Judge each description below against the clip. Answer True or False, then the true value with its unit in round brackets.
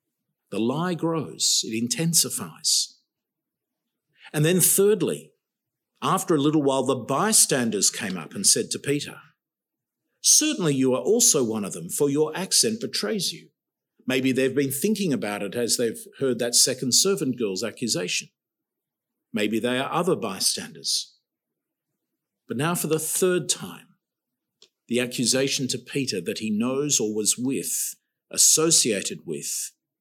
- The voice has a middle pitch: True (145 Hz)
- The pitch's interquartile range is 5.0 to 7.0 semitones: True (5.6 semitones)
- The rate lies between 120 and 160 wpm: True (140 wpm)